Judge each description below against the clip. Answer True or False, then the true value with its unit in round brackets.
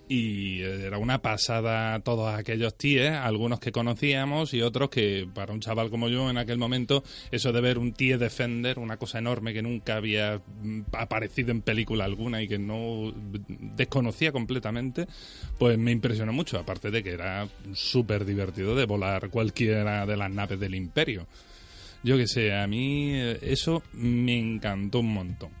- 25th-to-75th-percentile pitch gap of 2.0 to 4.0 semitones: True (3.1 semitones)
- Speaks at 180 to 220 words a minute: False (165 wpm)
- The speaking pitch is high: False (115 Hz)